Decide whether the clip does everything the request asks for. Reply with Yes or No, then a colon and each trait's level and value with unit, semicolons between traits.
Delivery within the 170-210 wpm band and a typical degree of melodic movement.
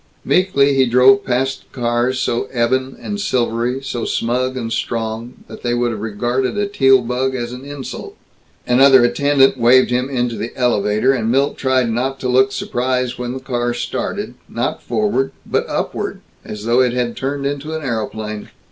No: average, 175 wpm; narrow, 1.9 semitones